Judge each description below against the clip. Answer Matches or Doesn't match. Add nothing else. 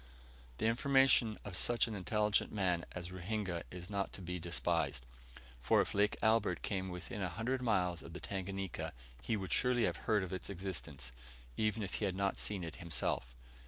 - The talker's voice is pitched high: Doesn't match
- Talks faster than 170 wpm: Matches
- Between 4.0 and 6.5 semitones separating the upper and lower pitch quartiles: Doesn't match